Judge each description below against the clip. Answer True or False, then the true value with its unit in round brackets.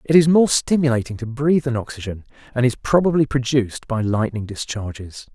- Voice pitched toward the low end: True (125 Hz)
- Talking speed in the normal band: True (170 wpm)